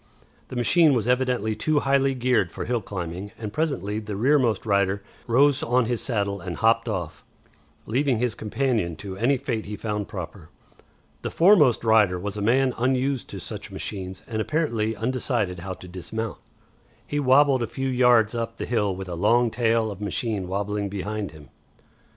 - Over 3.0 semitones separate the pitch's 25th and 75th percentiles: Yes, average, 4.1 semitones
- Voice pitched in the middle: No, low, 110 Hz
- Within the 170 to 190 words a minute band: Yes, average, 175 wpm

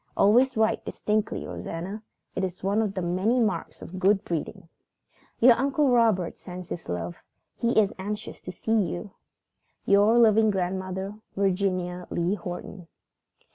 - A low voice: No, high, 195 Hz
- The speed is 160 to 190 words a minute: No, average, 140 wpm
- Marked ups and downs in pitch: No, average, 3.3 semitones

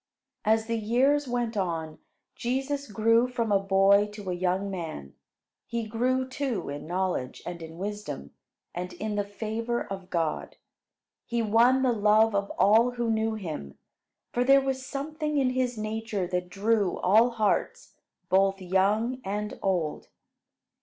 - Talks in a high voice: Yes, high, 215 Hz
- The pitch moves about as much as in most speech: Yes, average, 4.1 semitones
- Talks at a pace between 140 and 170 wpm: Yes, average, 150 wpm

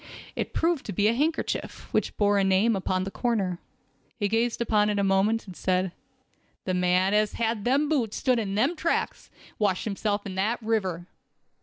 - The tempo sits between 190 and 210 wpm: Yes, average, 195 wpm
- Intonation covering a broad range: No, average, 3.3 semitones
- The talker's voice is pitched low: No, high, 210 Hz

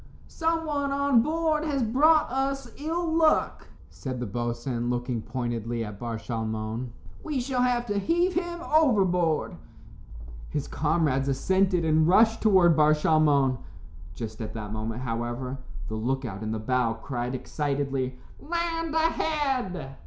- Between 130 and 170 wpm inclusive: Yes, average, 140 wpm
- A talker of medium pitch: Yes, medium, 155 Hz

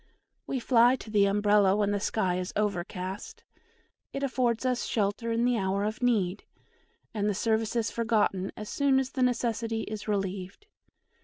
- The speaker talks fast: No, average, 165 wpm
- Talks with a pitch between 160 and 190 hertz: No, high, 215 Hz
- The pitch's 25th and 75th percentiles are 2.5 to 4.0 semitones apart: Yes, average, 3.1 semitones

